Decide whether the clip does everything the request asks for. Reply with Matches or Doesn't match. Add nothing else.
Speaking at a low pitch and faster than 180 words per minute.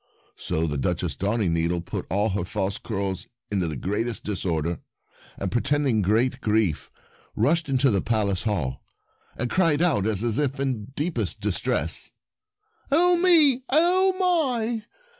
Doesn't match